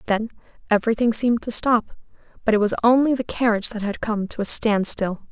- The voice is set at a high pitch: Yes, high, 220 Hz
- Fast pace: No, average, 190 wpm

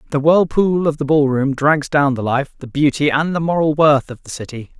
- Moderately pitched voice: Yes, medium, 145 Hz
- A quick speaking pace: Yes, fast, 240 wpm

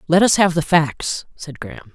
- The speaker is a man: Yes, male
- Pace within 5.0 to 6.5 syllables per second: No, 4.7 syllables/s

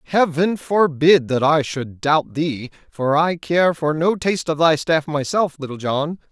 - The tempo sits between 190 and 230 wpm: No, average, 180 wpm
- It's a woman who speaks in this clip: No, male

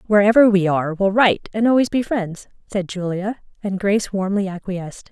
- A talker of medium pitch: No, high, 200 Hz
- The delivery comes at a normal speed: Yes, average, 175 wpm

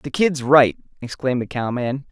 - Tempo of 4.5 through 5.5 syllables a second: Yes, 5.0 syllables/s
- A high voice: No, low, 130 Hz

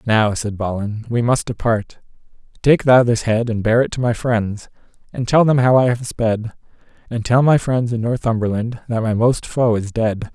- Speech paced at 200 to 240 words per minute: Yes, fast, 205 wpm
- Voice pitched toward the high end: No, low, 115 Hz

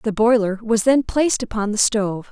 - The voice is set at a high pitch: Yes, high, 220 Hz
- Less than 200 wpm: No, fast, 205 wpm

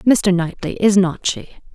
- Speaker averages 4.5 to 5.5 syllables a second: No, 4.1 syllables/s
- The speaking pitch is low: No, medium, 185 Hz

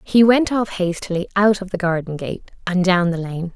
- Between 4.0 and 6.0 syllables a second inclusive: Yes, 5.0 syllables/s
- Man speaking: No, female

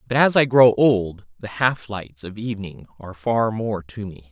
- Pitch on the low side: Yes, low, 110 Hz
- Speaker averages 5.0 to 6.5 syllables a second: No, 4.6 syllables/s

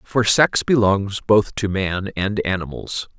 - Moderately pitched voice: No, low, 100 Hz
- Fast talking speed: No, average, 150 wpm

